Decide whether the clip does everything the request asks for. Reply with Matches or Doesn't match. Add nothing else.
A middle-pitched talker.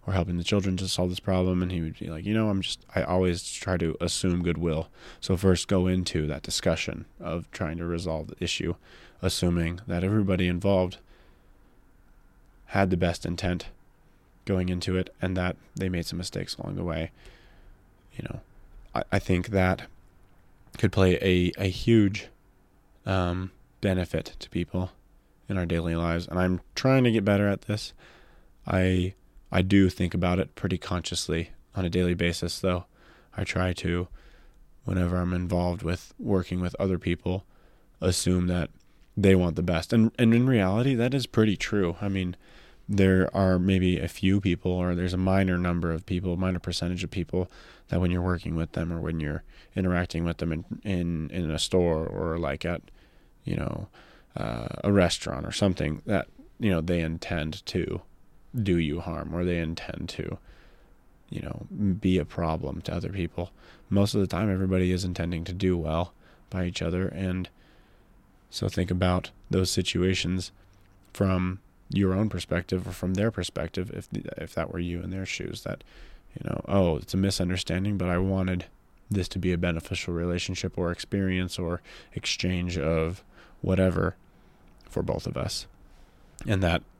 Doesn't match